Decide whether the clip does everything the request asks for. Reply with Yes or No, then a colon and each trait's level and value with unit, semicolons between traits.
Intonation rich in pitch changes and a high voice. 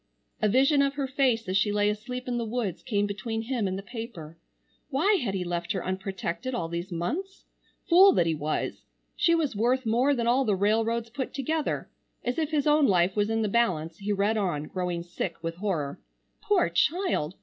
Yes: wide, 5.9 semitones; high, 220 Hz